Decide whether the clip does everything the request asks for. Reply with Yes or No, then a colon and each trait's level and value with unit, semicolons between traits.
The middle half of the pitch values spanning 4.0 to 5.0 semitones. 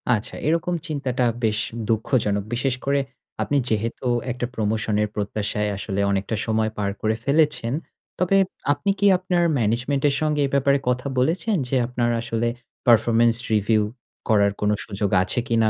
Yes: average, 4.5 semitones